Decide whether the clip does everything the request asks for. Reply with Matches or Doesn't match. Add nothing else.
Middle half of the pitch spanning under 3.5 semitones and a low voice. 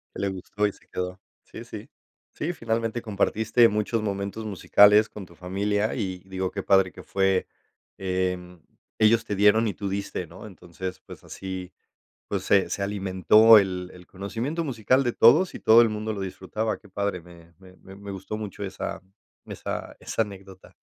Matches